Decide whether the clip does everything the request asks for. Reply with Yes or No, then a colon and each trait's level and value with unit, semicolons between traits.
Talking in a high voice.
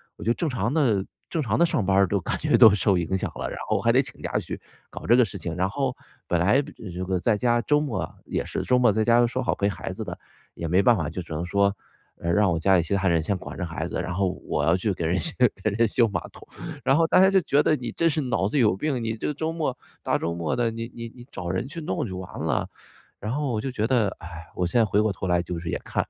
No: low, 105 Hz